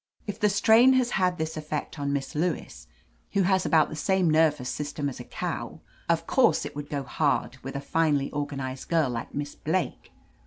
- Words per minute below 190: No, average, 200 wpm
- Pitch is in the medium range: Yes, medium, 155 Hz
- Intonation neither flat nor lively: Yes, average, 4.2 semitones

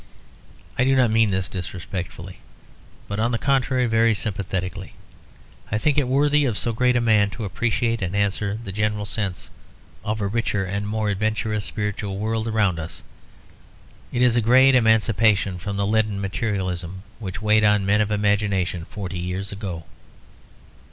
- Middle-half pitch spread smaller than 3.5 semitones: Yes, average, 2.7 semitones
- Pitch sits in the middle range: No, low, 105 Hz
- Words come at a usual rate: Yes, average, 160 wpm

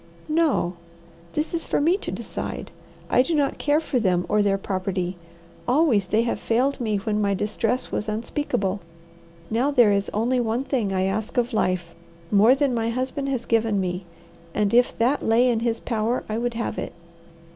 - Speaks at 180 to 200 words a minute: Yes, average, 185 wpm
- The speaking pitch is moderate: No, high, 230 Hz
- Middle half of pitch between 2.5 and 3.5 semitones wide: No, average, 4.0 semitones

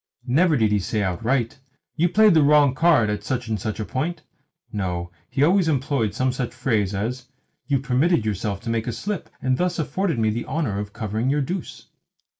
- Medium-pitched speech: No, low, 125 Hz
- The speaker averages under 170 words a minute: No, average, 200 wpm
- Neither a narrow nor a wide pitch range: No, wide, 5.7 semitones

